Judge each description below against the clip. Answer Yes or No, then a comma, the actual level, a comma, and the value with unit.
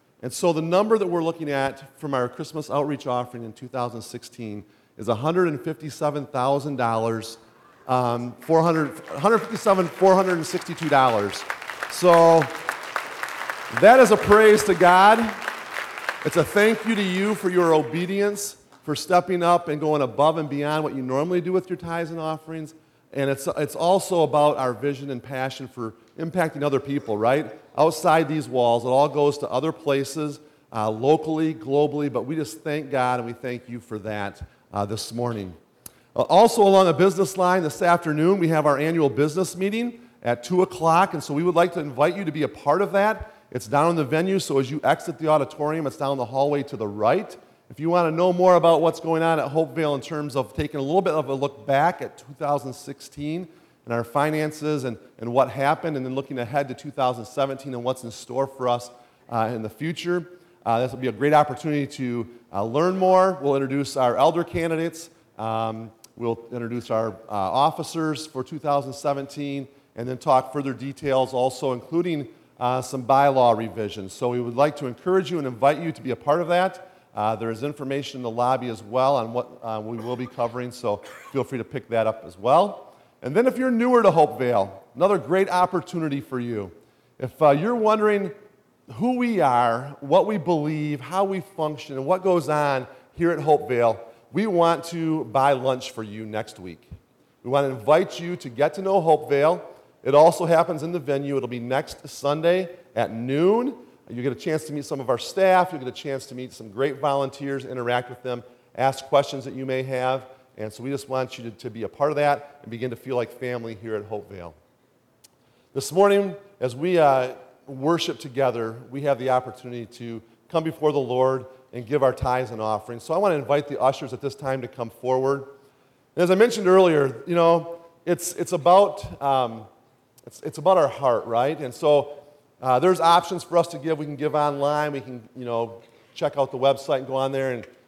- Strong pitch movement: No, average, 4.8 semitones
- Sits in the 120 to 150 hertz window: Yes, medium, 140 Hz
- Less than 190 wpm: No, average, 200 wpm